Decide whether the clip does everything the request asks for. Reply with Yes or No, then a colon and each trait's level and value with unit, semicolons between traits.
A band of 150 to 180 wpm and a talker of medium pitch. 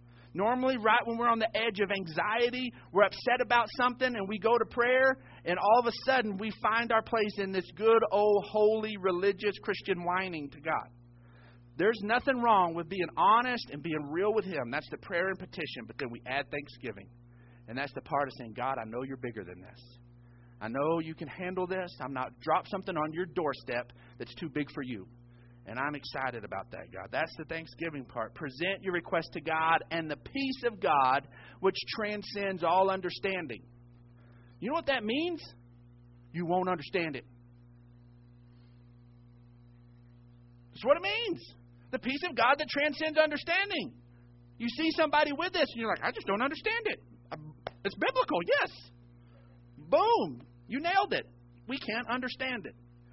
Yes: average, 175 wpm; medium, 165 Hz